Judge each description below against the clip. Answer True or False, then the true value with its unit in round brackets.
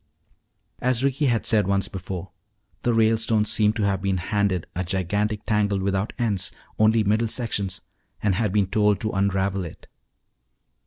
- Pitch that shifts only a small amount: True (2.3 semitones)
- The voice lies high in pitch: False (105 Hz)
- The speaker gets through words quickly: False (155 wpm)